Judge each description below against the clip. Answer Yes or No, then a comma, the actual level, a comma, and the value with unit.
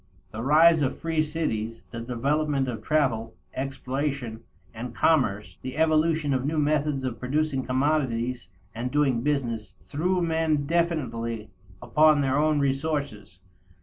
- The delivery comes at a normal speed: No, slow, 130 wpm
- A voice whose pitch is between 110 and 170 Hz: Yes, medium, 140 Hz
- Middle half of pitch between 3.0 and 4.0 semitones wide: No, average, 4.6 semitones